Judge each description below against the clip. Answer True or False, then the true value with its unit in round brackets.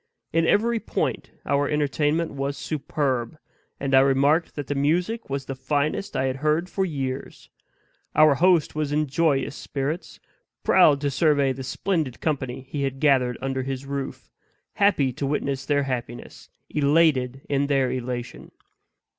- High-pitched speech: False (140 Hz)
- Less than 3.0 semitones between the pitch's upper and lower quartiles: True (2.5 semitones)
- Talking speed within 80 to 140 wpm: False (150 wpm)